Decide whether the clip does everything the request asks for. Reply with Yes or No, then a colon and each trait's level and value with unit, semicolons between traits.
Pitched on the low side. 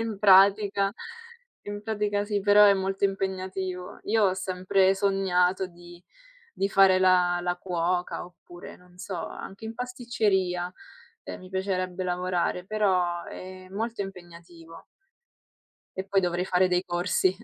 No: high, 190 Hz